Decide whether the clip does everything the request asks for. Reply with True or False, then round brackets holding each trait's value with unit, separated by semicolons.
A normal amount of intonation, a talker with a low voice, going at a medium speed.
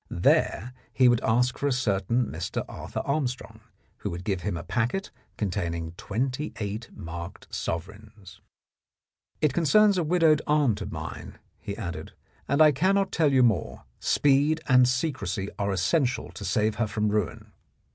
False (6.2 semitones; 120 Hz; 155 wpm)